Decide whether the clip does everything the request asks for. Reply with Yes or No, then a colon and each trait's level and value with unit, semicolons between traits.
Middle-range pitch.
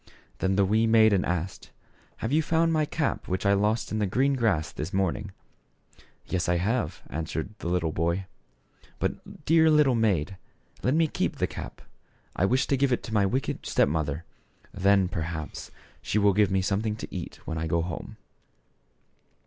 No: low, 100 Hz